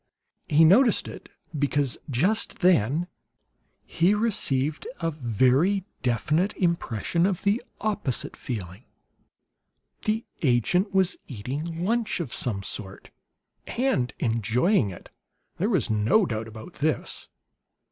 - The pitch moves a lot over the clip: Yes, wide, 8.0 semitones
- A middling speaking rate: No, slow, 110 wpm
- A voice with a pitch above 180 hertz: No, medium, 155 Hz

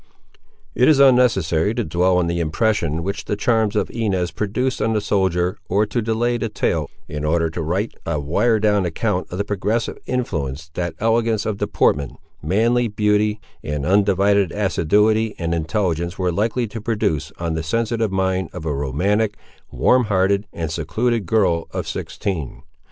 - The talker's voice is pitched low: Yes, low, 100 Hz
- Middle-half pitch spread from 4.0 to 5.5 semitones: Yes, average, 4.8 semitones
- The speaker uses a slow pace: No, average, 165 wpm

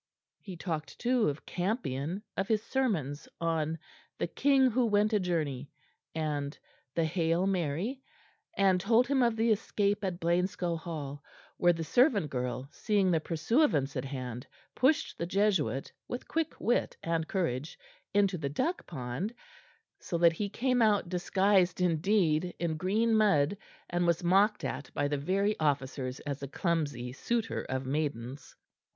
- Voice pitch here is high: No, medium, 175 Hz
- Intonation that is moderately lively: No, wide, 6.0 semitones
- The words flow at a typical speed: Yes, average, 155 wpm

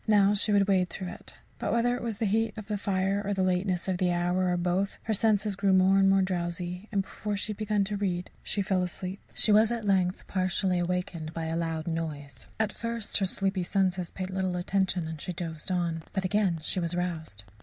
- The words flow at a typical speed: No, fast, 230 wpm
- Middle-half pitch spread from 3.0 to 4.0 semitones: No, narrow, 2.4 semitones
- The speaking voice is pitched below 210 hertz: Yes, medium, 185 Hz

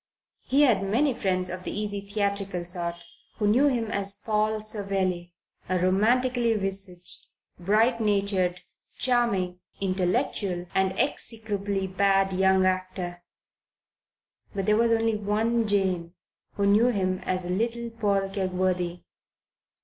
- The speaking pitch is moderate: No, high, 200 Hz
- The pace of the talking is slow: Yes, slow, 120 wpm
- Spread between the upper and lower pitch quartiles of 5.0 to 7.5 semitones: No, average, 2.9 semitones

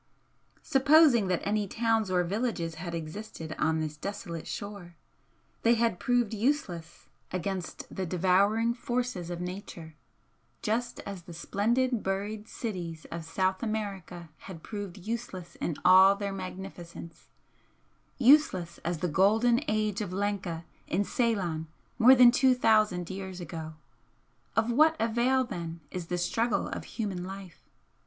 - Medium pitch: No, high, 195 Hz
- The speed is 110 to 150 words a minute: Yes, slow, 135 wpm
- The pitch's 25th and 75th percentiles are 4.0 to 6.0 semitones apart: Yes, average, 4.5 semitones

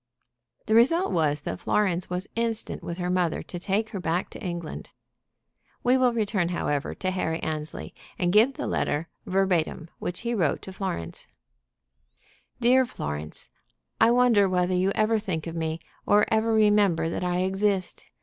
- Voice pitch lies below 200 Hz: Yes, medium, 185 Hz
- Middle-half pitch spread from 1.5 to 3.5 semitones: No, average, 4.4 semitones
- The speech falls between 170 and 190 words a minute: No, average, 160 wpm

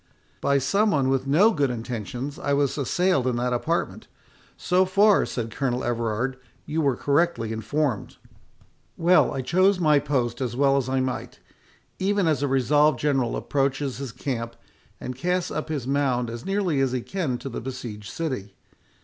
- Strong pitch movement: No, average, 4.1 semitones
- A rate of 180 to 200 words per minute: No, average, 170 wpm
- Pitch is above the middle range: No, low, 135 Hz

